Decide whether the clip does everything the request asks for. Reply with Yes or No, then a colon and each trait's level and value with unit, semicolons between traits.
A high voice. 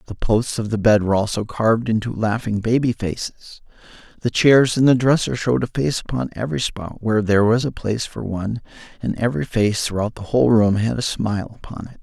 No: low, 110 Hz